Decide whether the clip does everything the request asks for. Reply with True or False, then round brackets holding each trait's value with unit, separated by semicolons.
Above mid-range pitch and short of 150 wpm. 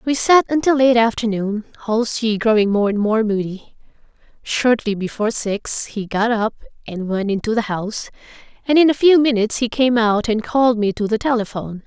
False (225 Hz; 180 wpm)